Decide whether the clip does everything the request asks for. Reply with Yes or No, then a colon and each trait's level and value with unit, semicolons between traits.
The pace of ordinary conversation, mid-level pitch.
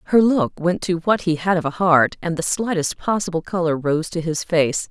No: fast, 230 wpm; medium, 170 Hz